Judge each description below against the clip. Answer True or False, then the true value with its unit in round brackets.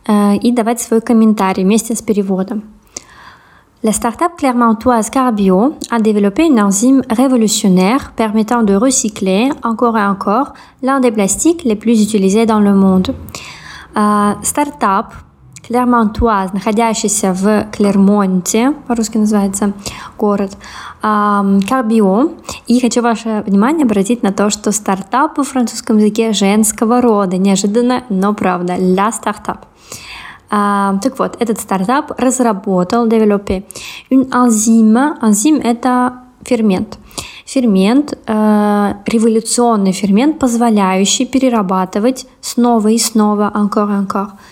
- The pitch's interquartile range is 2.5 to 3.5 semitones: True (3.2 semitones)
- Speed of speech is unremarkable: False (105 wpm)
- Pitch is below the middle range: False (220 Hz)